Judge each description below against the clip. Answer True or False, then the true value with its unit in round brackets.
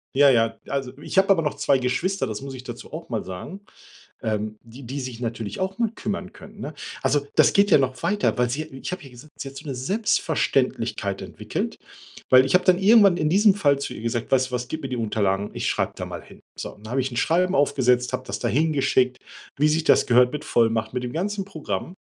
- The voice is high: False (135 Hz)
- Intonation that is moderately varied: False (6.5 semitones)